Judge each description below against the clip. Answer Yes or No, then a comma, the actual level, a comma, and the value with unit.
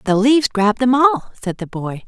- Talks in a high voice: Yes, high, 230 Hz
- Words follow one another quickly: Yes, fast, 230 wpm